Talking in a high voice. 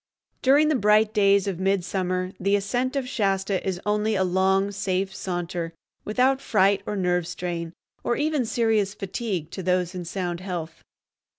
Yes: high, 195 Hz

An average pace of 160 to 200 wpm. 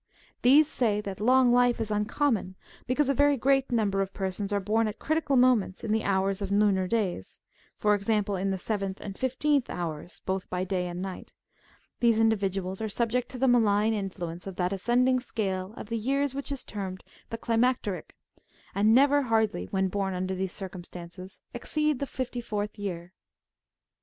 Yes: average, 190 wpm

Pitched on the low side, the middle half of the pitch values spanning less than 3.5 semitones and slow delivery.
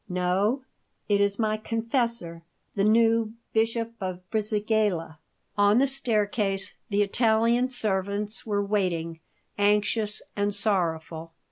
No: high, 210 Hz; average, 2.7 semitones; slow, 110 wpm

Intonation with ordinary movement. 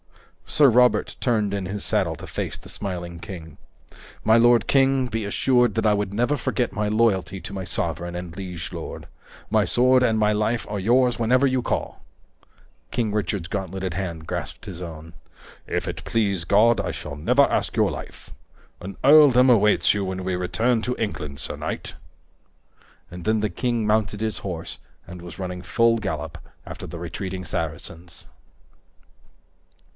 Yes: average, 4.6 semitones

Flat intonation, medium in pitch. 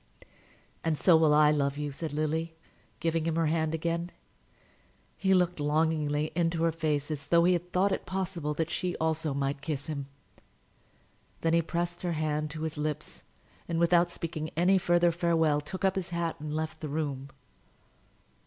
Yes: narrow, 2.1 semitones; medium, 160 Hz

